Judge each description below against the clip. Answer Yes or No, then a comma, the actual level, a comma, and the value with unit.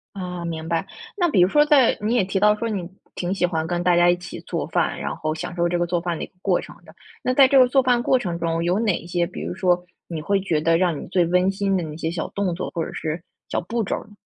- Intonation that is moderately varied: Yes, average, 3.1 semitones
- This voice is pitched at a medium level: Yes, medium, 180 Hz